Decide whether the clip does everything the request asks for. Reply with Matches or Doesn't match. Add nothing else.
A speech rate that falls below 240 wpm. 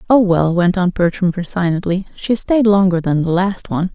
Matches